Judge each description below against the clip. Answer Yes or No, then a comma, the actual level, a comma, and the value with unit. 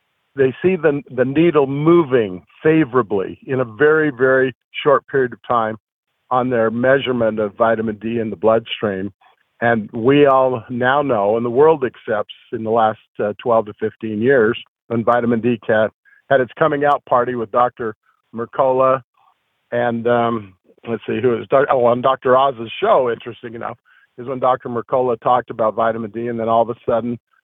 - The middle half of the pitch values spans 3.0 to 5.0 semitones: No, narrow, 2.6 semitones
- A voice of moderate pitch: No, low, 120 Hz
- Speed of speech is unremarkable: Yes, average, 175 wpm